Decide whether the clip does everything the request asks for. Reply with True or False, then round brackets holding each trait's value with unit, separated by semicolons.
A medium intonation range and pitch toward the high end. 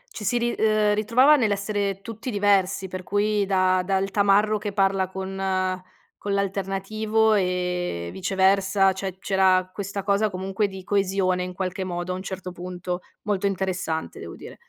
False (1.6 semitones; 195 Hz)